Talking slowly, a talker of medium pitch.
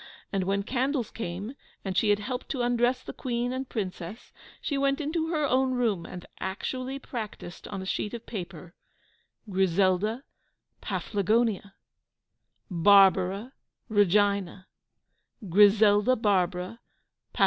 No: slow, 120 wpm; high, 210 Hz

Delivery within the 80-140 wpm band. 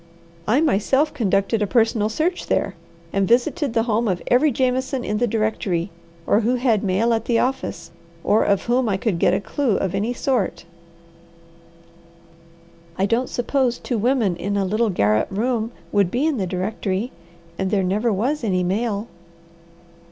No: average, 165 wpm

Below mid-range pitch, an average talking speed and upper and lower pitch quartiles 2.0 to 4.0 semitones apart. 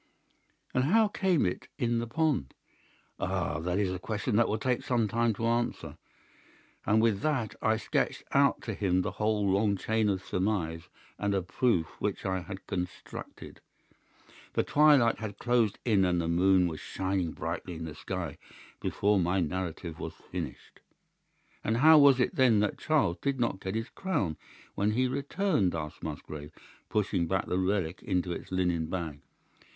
No: low, 100 Hz; average, 170 wpm; average, 4.7 semitones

